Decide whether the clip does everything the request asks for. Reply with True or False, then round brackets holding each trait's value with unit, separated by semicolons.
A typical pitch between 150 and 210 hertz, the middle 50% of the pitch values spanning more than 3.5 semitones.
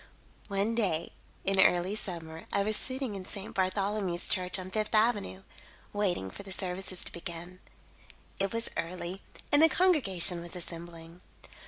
False (190 Hz; 3.1 semitones)